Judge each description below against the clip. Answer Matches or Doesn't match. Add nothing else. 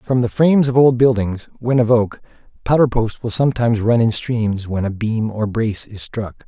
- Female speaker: Doesn't match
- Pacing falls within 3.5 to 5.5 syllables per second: Matches